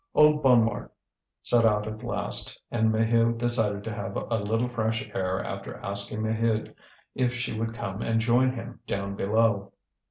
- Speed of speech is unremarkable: Yes, average, 160 wpm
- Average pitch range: No, narrow, 2.1 semitones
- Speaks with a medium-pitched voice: No, low, 115 Hz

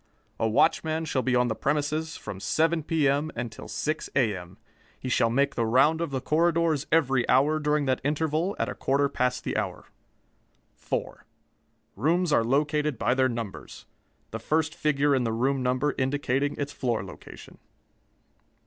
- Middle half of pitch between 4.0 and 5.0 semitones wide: No, average, 3.5 semitones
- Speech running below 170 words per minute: Yes, average, 160 wpm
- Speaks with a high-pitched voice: No, medium, 140 Hz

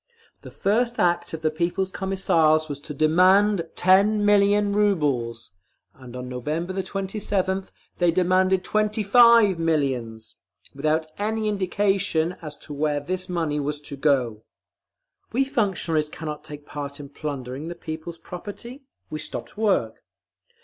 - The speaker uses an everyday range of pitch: Yes, average, 5.0 semitones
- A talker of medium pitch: Yes, medium, 170 Hz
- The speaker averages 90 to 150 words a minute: Yes, slow, 135 wpm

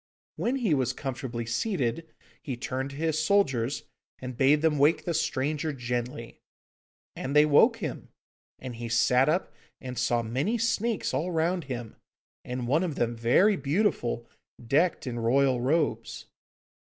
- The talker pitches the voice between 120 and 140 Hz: Yes, low, 135 Hz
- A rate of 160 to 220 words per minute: No, average, 150 wpm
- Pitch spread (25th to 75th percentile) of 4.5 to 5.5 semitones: Yes, average, 5.1 semitones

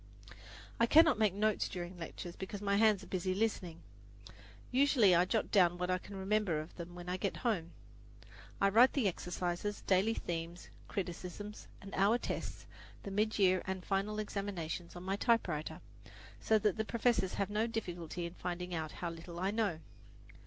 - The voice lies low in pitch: No, high, 190 Hz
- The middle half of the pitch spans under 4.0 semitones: Yes, average, 3.3 semitones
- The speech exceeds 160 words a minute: Yes, average, 175 wpm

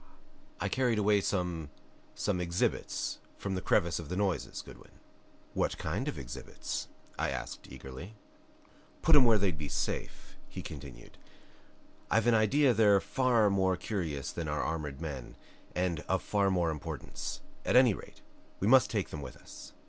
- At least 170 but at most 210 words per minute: No, average, 160 wpm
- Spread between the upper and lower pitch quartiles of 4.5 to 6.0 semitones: Yes, average, 5.0 semitones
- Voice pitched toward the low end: Yes, very low, 95 Hz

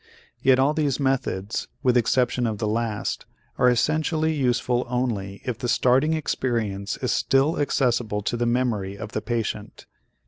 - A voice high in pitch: No, low, 125 Hz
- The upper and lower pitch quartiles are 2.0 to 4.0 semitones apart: Yes, average, 3.4 semitones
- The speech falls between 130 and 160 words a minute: Yes, average, 150 wpm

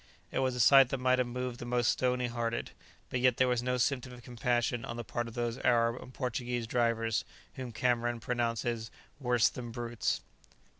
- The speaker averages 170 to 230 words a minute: Yes, average, 195 wpm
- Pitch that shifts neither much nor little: No, narrow, 1.3 semitones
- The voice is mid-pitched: No, low, 120 Hz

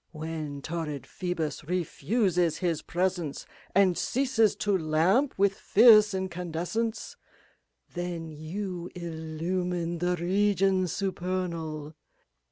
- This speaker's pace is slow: Yes, slow, 90 wpm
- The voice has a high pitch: No, medium, 180 Hz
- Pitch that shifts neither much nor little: Yes, average, 3.0 semitones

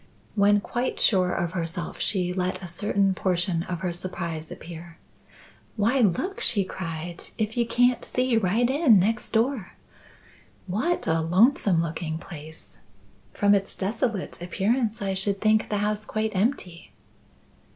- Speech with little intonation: No, average, 4.1 semitones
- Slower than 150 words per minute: Yes, average, 140 wpm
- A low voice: No, high, 195 Hz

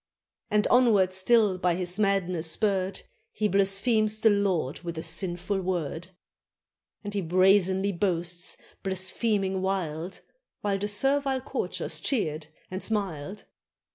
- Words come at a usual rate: No, slow, 120 wpm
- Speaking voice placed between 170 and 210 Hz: Yes, high, 190 Hz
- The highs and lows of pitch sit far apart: No, average, 2.7 semitones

